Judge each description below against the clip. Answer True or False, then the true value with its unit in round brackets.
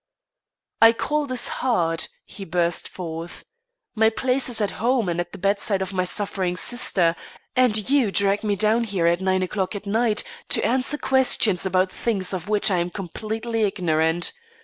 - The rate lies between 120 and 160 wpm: False (170 wpm)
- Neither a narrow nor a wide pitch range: True (4.1 semitones)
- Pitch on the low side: False (200 Hz)